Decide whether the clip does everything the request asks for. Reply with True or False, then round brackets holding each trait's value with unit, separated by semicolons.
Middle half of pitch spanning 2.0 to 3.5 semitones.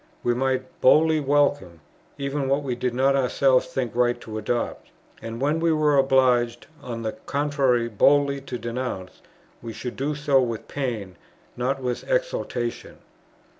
True (2.8 semitones)